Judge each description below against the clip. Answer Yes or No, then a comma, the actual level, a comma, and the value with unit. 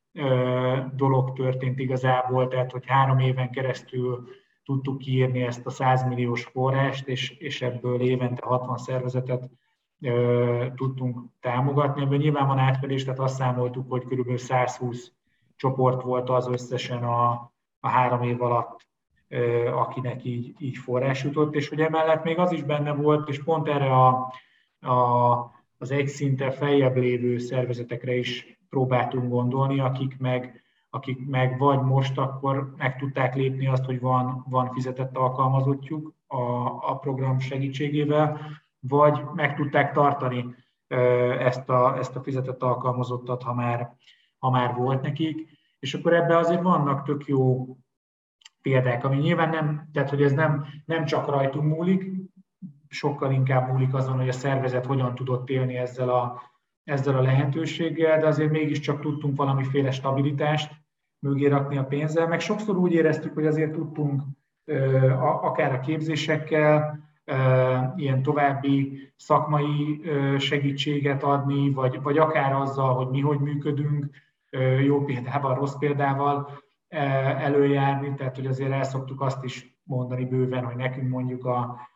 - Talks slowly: No, average, 140 wpm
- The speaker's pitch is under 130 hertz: No, low, 135 Hz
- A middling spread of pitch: No, narrow, 2.3 semitones